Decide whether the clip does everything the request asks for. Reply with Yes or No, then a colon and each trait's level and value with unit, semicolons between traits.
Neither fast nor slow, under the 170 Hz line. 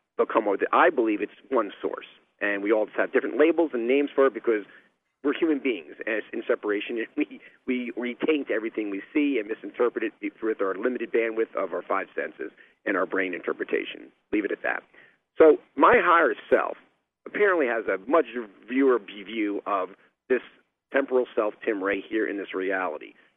Yes: average, 180 wpm; low, 135 Hz